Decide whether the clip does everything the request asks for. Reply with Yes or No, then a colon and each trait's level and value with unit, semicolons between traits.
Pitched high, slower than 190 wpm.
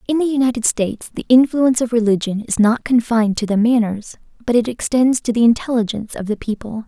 No: high, 230 Hz; average, 200 wpm